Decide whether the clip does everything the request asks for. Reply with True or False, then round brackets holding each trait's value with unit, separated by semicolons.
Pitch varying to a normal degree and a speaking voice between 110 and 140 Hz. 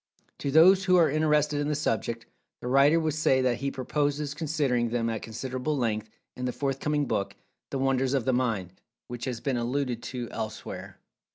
True (3.6 semitones; 135 Hz)